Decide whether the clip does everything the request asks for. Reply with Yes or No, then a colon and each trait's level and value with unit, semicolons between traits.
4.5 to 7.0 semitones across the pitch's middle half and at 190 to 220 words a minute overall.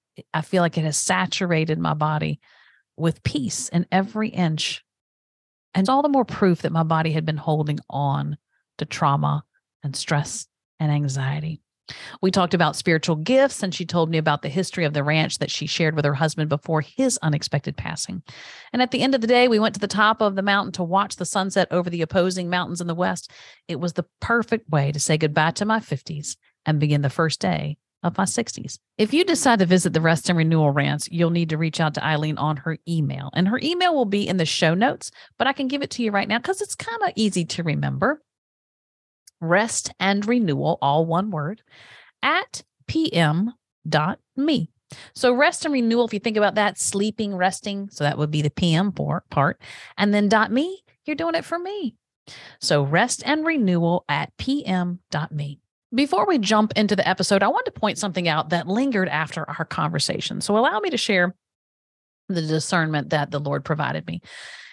Yes: wide, 5.5 semitones; average, 200 wpm